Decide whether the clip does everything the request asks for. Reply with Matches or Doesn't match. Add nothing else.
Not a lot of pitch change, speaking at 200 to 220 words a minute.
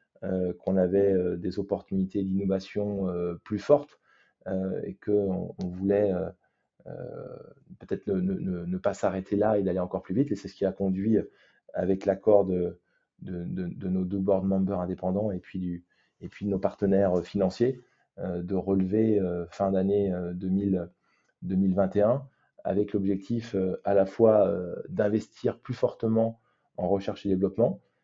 Doesn't match